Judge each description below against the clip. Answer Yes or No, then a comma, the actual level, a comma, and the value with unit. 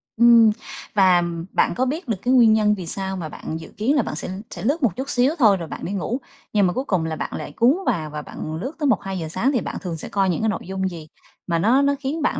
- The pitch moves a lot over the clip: Yes, wide, 6.3 semitones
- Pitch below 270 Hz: Yes, high, 210 Hz